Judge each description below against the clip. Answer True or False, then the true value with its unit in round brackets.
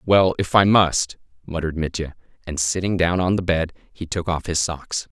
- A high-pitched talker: False (85 Hz)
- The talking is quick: False (195 wpm)